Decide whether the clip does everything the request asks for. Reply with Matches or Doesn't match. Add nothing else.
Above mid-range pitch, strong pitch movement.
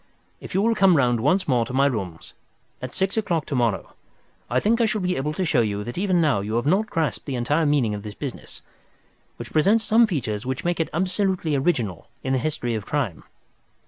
Doesn't match